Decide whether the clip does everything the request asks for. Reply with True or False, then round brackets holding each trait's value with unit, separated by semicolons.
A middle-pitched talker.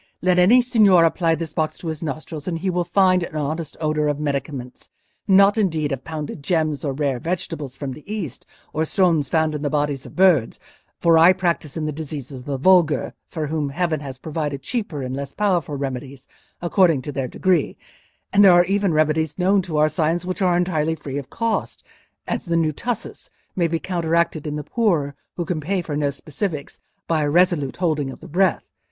True (160 Hz)